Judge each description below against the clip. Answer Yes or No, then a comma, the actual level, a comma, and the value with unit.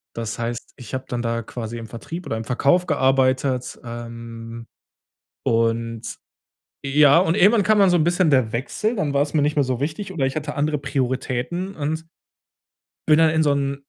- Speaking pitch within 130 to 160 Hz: Yes, low, 135 Hz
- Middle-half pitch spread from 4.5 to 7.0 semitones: Yes, average, 5.1 semitones